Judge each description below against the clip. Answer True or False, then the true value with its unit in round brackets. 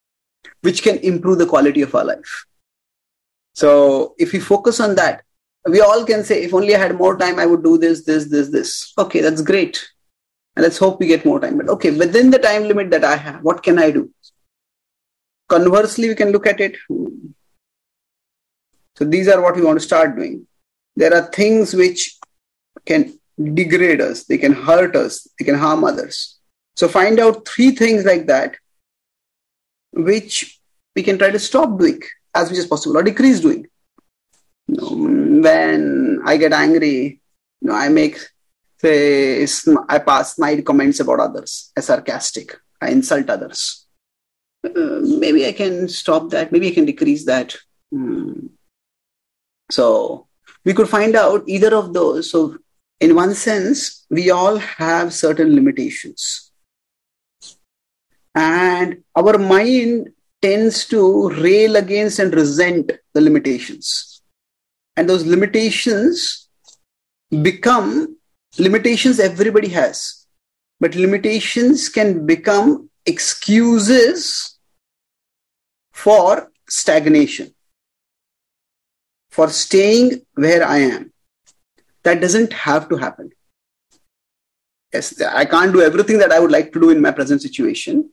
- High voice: True (210 Hz)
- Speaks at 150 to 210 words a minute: False (140 wpm)